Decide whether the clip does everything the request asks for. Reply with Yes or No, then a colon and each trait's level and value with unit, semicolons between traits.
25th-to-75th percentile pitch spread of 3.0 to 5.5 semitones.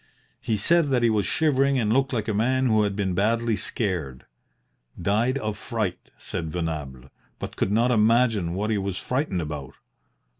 Yes: average, 4.8 semitones